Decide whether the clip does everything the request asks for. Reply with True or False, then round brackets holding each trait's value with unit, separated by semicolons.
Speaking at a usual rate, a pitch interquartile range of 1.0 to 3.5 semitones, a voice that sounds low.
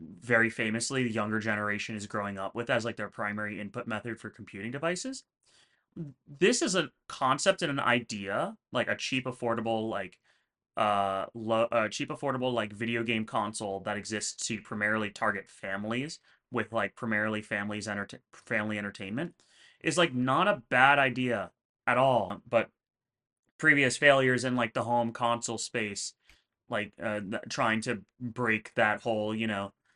True (155 wpm; 3.1 semitones; 115 Hz)